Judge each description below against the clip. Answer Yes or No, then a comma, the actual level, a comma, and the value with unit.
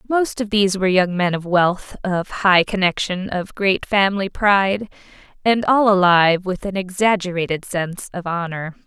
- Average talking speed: Yes, average, 160 wpm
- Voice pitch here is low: No, high, 190 Hz